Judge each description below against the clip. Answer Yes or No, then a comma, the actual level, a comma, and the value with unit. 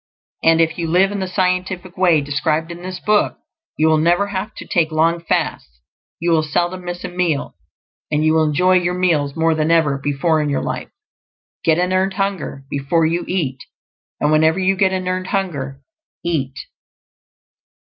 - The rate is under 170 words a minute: No, average, 180 wpm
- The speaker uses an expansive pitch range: No, average, 2.9 semitones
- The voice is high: No, medium, 170 Hz